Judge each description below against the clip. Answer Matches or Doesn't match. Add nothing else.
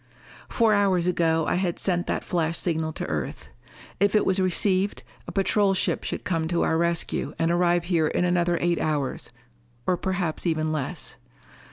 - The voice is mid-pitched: Matches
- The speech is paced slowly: Doesn't match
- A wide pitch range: Doesn't match